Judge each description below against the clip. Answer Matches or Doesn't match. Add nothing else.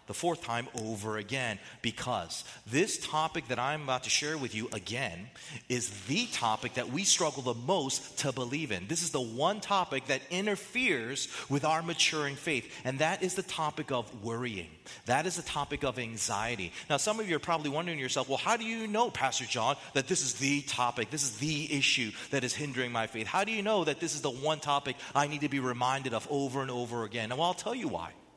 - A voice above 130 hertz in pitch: Matches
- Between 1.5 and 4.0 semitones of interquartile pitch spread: Doesn't match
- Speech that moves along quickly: Matches